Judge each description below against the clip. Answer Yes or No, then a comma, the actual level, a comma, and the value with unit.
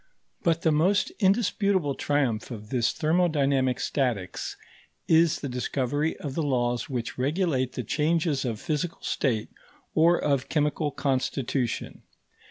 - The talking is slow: Yes, slow, 125 wpm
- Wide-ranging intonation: No, average, 4.1 semitones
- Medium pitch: Yes, medium, 145 Hz